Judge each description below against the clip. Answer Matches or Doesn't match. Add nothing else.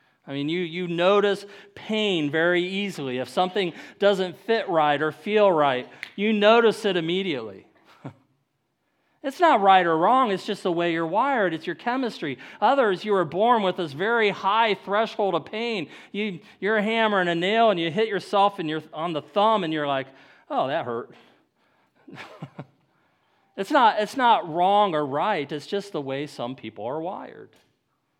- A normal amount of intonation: Matches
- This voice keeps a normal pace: Matches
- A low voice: Doesn't match